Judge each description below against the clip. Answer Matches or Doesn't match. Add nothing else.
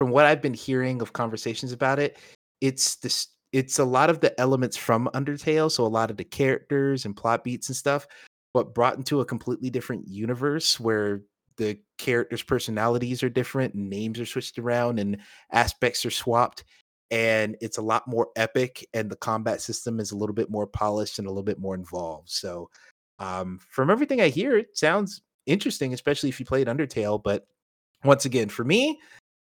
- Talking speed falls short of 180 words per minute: Doesn't match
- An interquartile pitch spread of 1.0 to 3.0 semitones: Doesn't match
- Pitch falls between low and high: Doesn't match